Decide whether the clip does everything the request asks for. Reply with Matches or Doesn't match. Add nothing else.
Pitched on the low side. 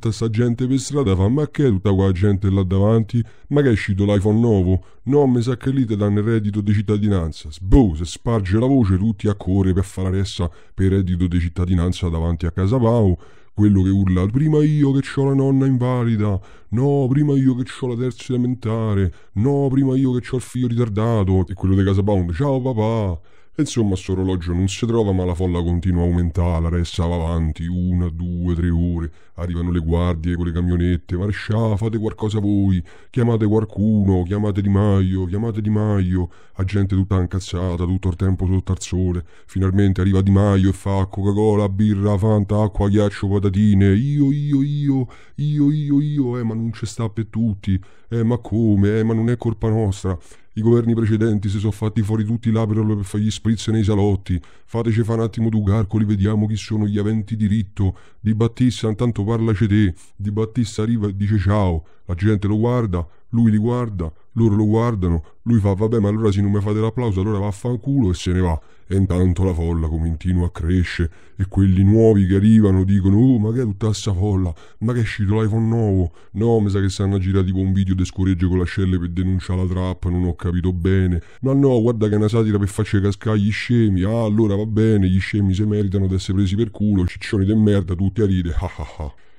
Matches